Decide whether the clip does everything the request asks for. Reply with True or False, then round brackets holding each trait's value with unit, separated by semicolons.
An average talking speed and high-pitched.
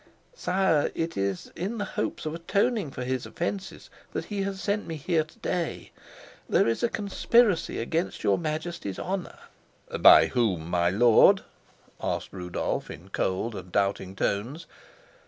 False (150 wpm; 155 Hz)